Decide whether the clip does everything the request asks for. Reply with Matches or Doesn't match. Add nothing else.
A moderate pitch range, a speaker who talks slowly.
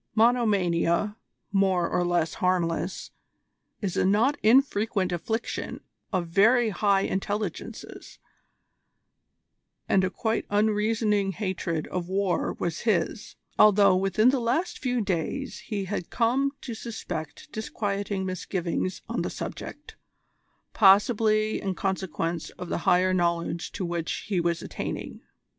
Matches